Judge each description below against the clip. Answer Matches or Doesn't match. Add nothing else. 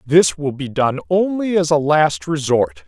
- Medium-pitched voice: Matches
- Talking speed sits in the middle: Matches